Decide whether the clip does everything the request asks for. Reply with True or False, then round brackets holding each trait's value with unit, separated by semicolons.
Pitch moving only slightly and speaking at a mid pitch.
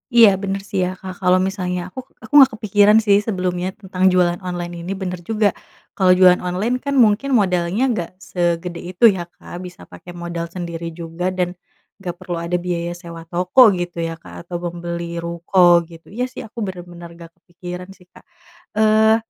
True (2.3 semitones; 180 Hz)